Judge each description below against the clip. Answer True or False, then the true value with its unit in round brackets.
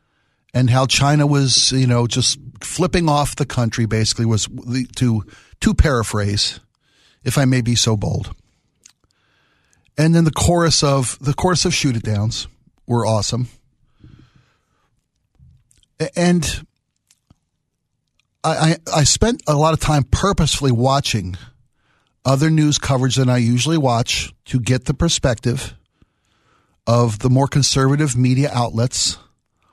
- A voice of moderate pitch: False (130 Hz)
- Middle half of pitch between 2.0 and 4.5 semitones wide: True (3.7 semitones)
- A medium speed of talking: False (120 wpm)